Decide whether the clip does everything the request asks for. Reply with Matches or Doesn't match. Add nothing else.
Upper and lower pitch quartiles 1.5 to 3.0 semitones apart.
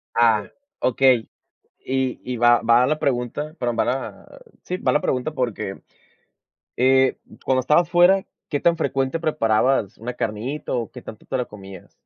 Doesn't match